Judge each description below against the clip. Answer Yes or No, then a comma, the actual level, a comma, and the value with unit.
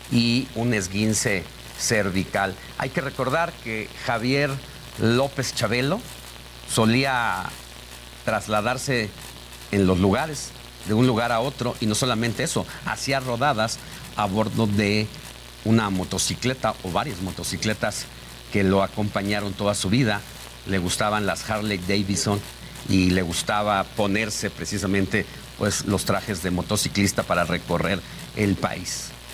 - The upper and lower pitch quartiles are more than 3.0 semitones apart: Yes, average, 4.1 semitones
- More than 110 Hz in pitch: No, low, 105 Hz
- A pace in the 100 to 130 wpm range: Yes, slow, 125 wpm